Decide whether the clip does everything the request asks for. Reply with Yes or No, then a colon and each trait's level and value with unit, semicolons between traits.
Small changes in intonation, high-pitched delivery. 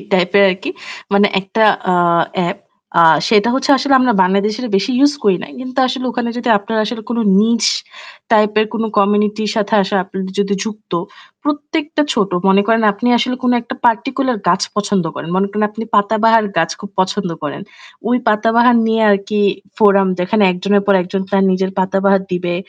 No: average, 3.2 semitones; high, 210 Hz